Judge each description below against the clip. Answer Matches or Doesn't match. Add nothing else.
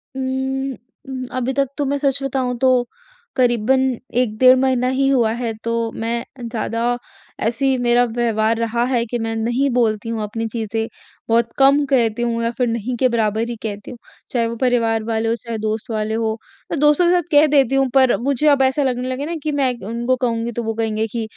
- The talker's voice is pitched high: Matches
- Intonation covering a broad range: Doesn't match